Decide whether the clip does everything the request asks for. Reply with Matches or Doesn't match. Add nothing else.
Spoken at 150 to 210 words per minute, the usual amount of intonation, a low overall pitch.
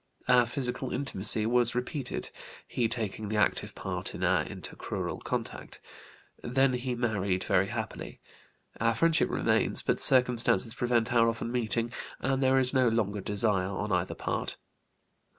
Doesn't match